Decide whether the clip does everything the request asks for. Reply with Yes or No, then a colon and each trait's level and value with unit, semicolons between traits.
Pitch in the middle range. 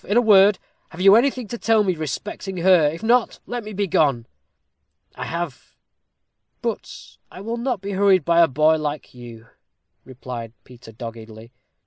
Yes: medium, 175 Hz